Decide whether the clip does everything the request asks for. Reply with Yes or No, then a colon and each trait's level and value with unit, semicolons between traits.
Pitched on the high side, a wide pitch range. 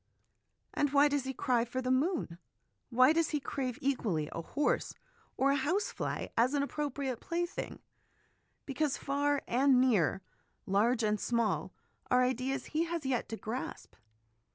No: very high, 265 Hz; average, 3.3 semitones